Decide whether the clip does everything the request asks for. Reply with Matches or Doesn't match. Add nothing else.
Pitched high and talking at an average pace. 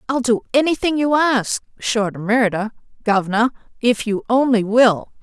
Matches